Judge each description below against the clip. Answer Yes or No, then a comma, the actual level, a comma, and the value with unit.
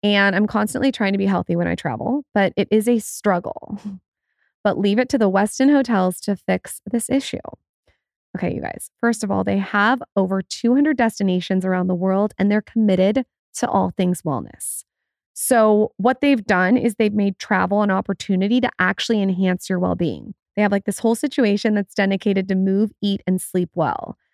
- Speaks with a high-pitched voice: Yes, high, 205 Hz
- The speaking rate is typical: Yes, average, 190 wpm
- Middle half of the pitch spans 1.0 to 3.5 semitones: Yes, average, 3.2 semitones